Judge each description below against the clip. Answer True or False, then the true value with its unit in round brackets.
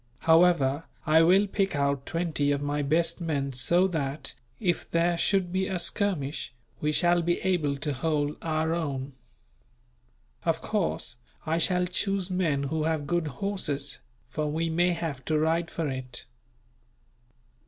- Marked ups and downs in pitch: False (3.4 semitones)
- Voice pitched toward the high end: False (160 Hz)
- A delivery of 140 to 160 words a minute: True (150 wpm)